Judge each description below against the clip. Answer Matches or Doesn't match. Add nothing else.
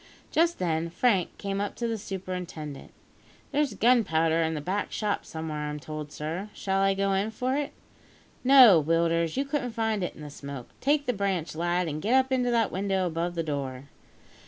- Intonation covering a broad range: Matches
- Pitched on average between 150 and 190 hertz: Matches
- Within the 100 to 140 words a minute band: Doesn't match